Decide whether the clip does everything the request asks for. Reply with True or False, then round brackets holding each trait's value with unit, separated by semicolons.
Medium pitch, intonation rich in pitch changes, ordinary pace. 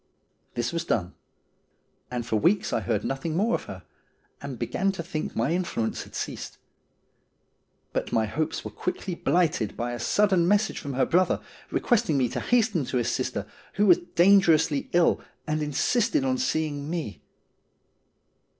True (165 Hz; 6.7 semitones; 160 wpm)